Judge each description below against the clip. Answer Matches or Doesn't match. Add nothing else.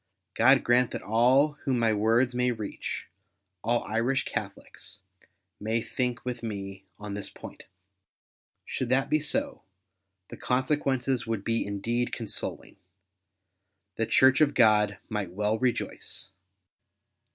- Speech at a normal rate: Doesn't match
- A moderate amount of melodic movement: Matches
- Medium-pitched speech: Doesn't match